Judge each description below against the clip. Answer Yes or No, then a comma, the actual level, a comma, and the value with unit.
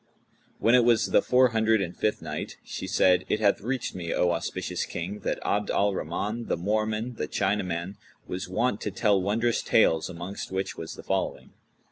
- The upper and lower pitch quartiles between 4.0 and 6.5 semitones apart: No, average, 3.5 semitones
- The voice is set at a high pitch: No, low, 100 Hz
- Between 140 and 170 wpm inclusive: No, average, 185 wpm